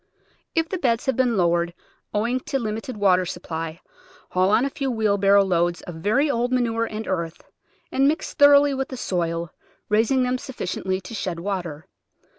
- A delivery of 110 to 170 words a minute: No, average, 180 wpm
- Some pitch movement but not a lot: No, wide, 6.1 semitones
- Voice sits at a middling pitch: No, high, 215 Hz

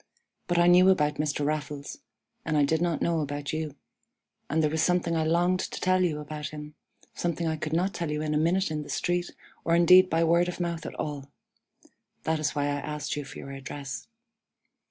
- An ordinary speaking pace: No, fast, 215 wpm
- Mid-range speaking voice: Yes, medium, 155 Hz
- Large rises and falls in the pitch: No, narrow, 2.6 semitones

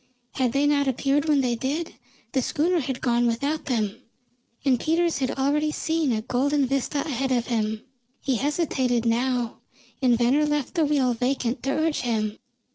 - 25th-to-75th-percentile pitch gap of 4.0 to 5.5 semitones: No, average, 3.4 semitones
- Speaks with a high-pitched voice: Yes, very high, 265 Hz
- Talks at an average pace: Yes, average, 170 wpm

